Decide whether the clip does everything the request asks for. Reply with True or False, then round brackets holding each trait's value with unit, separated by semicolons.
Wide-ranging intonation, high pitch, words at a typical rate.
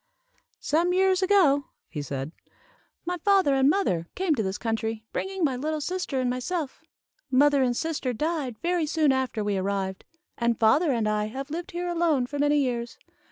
True (6.6 semitones; 280 Hz; 175 wpm)